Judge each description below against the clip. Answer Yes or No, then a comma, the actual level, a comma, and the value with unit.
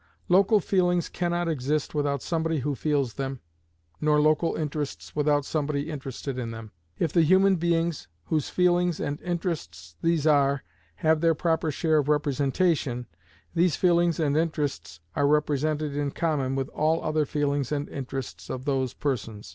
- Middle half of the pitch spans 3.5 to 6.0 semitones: No, average, 3.1 semitones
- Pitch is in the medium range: Yes, medium, 150 Hz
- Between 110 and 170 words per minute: Yes, average, 155 wpm